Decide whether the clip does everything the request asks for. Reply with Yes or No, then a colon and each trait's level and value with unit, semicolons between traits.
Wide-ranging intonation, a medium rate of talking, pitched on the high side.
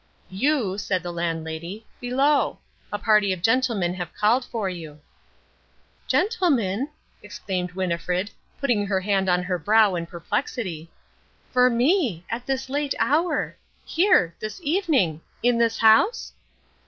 No: wide, 6.4 semitones; slow, 130 wpm; high, 210 Hz